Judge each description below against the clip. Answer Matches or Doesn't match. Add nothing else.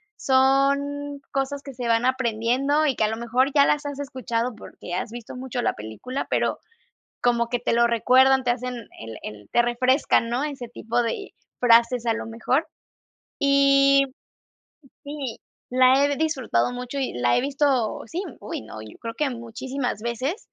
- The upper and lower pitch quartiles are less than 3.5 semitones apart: Matches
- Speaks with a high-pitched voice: Matches